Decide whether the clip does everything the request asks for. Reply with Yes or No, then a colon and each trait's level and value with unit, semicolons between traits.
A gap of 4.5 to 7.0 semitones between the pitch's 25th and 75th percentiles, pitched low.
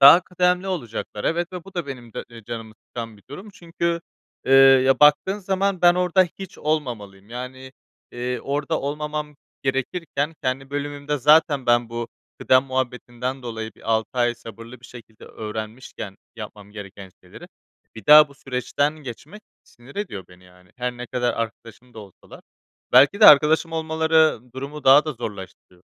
Yes: average, 5.0 semitones; low, 130 Hz